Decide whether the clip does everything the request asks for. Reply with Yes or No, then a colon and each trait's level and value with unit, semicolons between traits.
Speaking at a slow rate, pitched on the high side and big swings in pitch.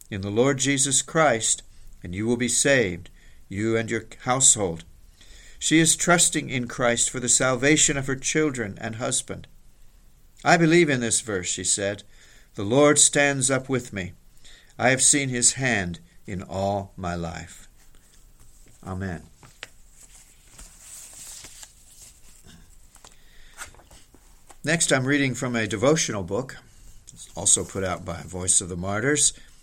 No: slow, 130 wpm; low, 115 Hz; wide, 6.6 semitones